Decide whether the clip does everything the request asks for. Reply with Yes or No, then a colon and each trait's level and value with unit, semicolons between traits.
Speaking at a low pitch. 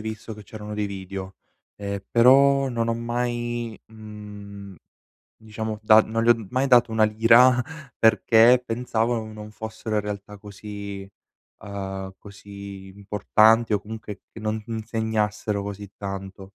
Yes: low, 110 Hz